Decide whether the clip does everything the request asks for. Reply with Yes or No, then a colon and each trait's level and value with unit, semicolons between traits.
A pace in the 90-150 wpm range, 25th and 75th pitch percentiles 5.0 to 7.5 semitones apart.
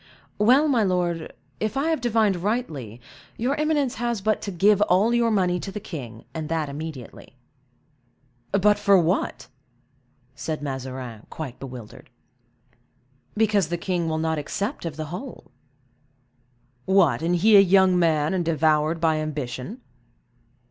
Yes: average, 140 wpm; wide, 5.4 semitones